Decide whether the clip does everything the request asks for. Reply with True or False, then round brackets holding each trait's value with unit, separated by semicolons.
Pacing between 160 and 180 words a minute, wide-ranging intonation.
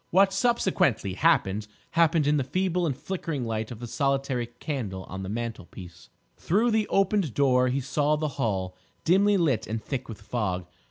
True (170 wpm; 7.3 semitones)